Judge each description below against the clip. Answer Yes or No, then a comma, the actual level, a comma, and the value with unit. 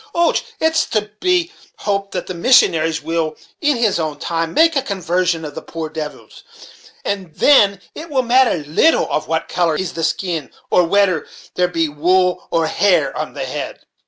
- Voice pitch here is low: No, medium, 180 Hz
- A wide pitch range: No, average, 4.9 semitones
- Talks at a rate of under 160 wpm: No, average, 180 wpm